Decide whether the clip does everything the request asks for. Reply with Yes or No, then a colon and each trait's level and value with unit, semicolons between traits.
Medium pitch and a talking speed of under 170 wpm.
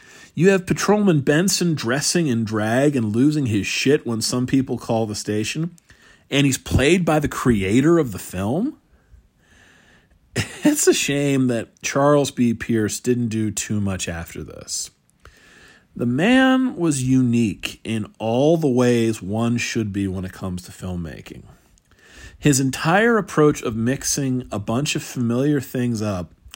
No: low, 125 Hz; average, 150 wpm